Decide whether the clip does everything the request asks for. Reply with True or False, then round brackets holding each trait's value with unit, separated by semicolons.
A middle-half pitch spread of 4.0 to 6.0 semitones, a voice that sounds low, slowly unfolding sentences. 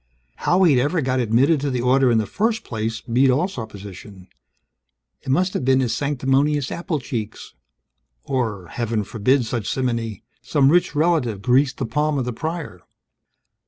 False (4.4 semitones; 130 Hz; 160 wpm)